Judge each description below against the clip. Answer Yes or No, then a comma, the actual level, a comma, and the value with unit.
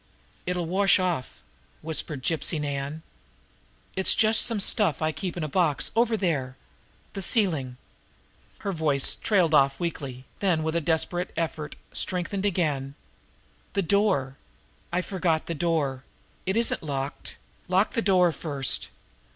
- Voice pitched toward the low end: No, medium, 165 Hz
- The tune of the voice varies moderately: Yes, average, 4.7 semitones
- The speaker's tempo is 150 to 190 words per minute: No, average, 140 wpm